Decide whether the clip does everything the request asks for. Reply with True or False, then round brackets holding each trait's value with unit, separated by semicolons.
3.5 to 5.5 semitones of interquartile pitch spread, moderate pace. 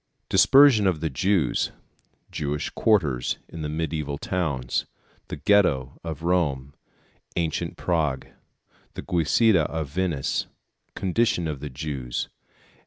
False (4.5 semitones; 110 wpm)